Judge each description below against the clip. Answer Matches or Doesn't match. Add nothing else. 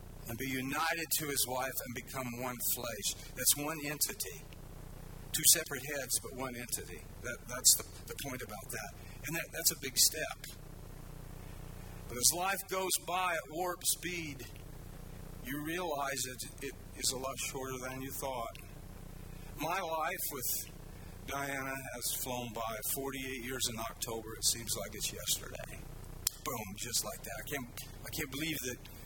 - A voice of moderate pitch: Doesn't match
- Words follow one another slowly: Doesn't match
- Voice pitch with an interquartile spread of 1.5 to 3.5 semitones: Matches